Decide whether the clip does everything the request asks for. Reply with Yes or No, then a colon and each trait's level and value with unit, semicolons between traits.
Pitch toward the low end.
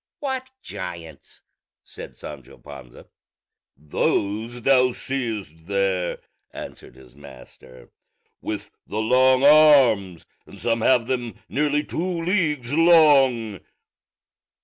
Yes: low, 120 Hz